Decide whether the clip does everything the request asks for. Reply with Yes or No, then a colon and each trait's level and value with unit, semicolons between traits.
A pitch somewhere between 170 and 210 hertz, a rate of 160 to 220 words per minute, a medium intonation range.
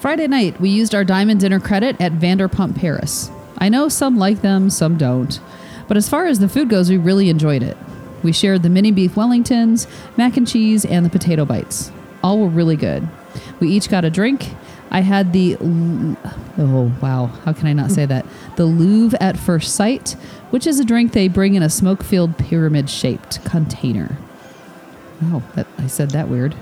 Yes: medium, 185 Hz; average, 195 wpm; average, 4.9 semitones